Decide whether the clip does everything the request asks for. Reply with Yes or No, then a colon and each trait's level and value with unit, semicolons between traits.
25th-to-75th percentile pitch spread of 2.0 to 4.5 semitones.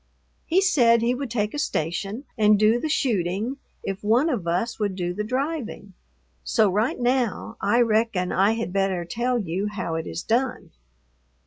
Yes: average, 4.1 semitones